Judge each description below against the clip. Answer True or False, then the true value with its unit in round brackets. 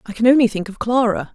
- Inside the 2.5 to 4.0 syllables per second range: False (6.5 syllables/s)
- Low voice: False (225 Hz)